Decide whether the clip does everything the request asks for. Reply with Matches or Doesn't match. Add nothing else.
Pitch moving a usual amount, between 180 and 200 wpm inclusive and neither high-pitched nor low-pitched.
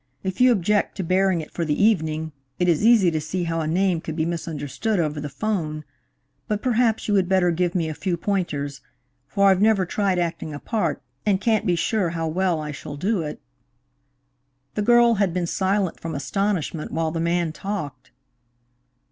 Matches